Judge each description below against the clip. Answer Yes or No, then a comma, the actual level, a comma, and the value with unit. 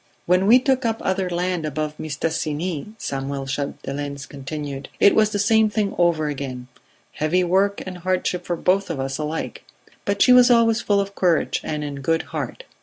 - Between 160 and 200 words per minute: Yes, average, 180 wpm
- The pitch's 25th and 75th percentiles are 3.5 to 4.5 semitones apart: No, wide, 5.4 semitones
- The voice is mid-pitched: Yes, medium, 175 Hz